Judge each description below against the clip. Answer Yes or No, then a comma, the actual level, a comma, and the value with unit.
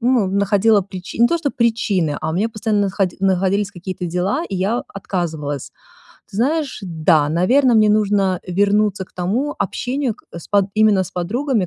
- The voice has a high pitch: Yes, high, 200 Hz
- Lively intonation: No, average, 3.8 semitones